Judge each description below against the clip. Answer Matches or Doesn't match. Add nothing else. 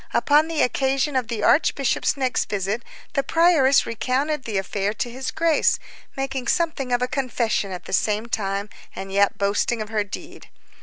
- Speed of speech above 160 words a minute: Matches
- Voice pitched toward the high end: Matches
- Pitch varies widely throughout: Doesn't match